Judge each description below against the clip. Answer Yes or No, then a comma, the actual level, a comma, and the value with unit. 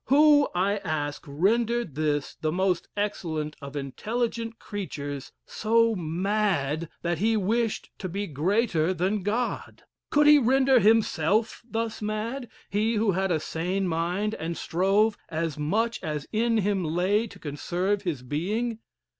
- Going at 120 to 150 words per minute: Yes, average, 140 wpm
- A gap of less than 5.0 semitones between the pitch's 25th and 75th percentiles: No, wide, 5.6 semitones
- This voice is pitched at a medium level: No, high, 195 Hz